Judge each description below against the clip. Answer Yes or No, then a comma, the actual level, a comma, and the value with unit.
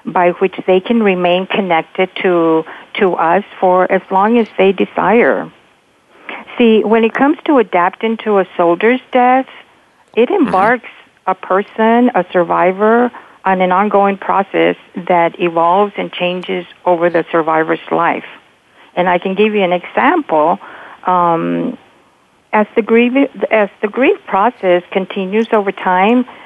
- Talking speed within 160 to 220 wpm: No, average, 140 wpm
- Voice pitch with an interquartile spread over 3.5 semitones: Yes, average, 3.9 semitones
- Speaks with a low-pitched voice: No, high, 195 Hz